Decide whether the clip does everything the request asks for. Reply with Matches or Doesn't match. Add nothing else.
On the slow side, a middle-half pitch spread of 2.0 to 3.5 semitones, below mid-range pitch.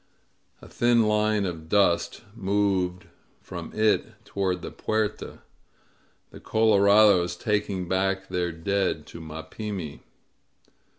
Matches